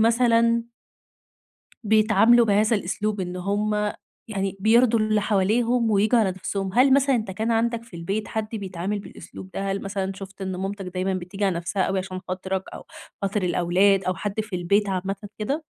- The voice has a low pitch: No, high, 200 Hz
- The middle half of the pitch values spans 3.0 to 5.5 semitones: No, narrow, 2.6 semitones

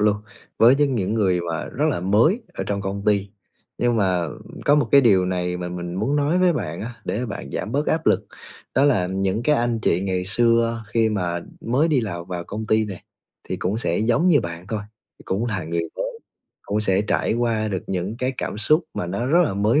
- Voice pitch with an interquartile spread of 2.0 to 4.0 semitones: No, average, 4.7 semitones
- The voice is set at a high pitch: No, low, 105 Hz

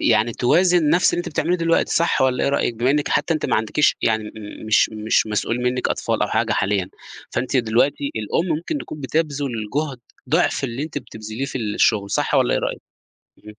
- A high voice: No, low, 130 Hz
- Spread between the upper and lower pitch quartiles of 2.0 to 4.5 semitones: No, wide, 5.6 semitones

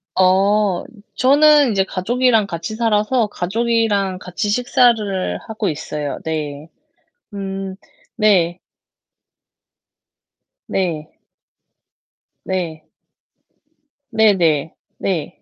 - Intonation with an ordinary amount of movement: Yes, average, 4.1 semitones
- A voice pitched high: Yes, high, 195 Hz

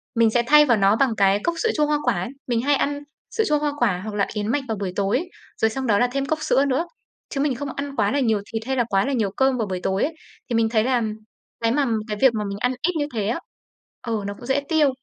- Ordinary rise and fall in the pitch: Yes, average, 4.9 semitones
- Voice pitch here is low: No, high, 245 Hz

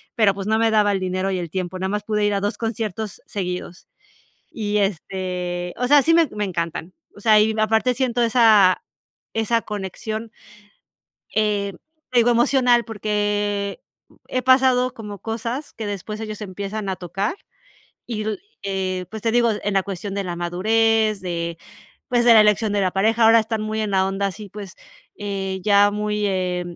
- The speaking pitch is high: Yes, high, 210 Hz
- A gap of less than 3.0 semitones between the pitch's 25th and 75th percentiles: Yes, narrow, 2.6 semitones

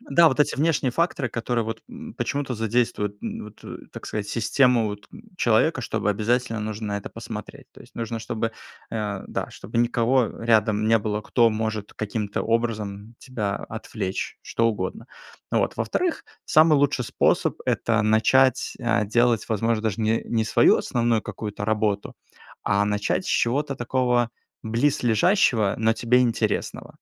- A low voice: Yes, low, 115 Hz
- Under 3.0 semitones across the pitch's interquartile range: Yes, narrow, 2.6 semitones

